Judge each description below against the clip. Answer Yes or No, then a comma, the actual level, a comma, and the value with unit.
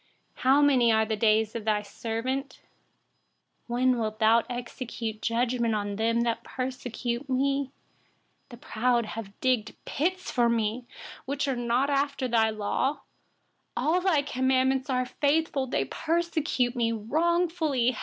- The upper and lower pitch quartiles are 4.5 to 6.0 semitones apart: No, average, 3.3 semitones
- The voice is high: Yes, very high, 250 Hz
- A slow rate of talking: Yes, slow, 130 wpm